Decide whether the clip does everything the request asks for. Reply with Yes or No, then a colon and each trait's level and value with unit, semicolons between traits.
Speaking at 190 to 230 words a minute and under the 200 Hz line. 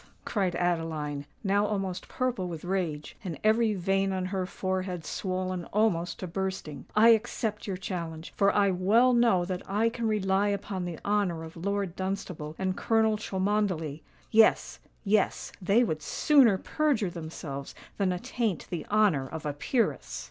No: average, 150 wpm; high, 190 Hz